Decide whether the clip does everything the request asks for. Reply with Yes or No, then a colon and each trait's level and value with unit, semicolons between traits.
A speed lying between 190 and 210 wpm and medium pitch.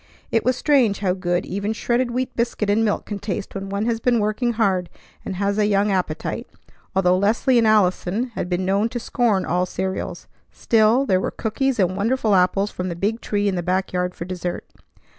No: fast, 205 wpm; high, 205 Hz